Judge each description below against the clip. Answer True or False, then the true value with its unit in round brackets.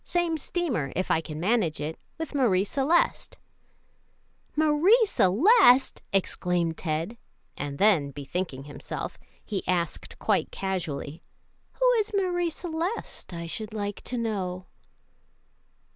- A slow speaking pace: True (115 wpm)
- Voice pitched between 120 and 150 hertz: False (200 Hz)